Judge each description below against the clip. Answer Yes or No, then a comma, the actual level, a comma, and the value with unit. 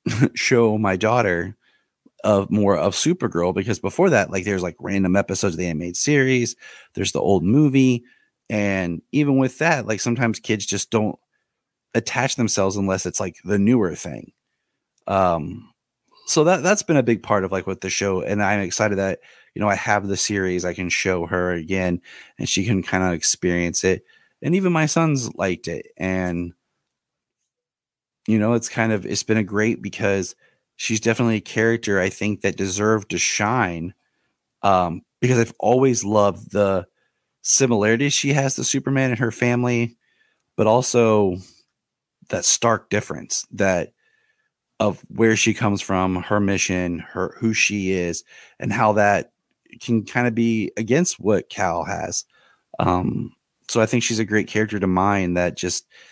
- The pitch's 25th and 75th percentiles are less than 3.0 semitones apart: No, average, 3.8 semitones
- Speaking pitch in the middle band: No, low, 105 Hz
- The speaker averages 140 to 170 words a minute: Yes, average, 165 wpm